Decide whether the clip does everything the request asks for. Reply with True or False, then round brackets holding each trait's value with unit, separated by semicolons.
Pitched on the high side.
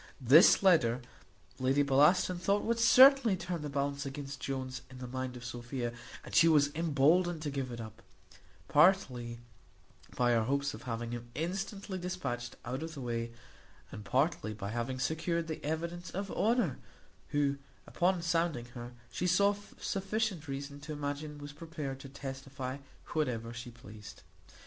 False (145 Hz)